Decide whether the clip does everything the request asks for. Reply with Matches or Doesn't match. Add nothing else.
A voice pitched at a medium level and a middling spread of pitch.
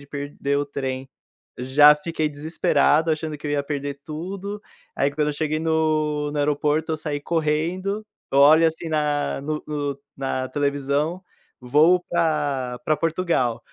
Doesn't match